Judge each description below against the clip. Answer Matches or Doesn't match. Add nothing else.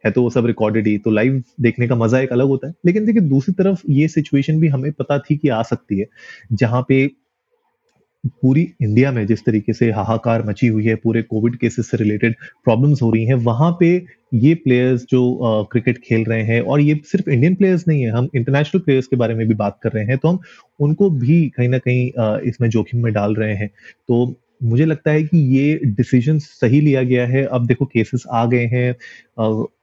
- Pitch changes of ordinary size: Matches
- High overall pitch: Doesn't match